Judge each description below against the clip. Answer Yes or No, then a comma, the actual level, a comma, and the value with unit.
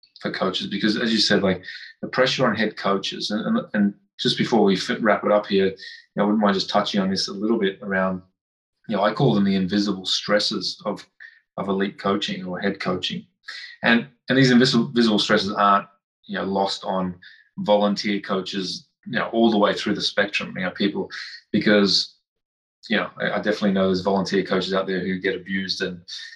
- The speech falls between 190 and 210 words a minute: Yes, fast, 205 wpm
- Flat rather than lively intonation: Yes, narrow, 1.7 semitones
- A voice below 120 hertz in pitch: Yes, low, 100 Hz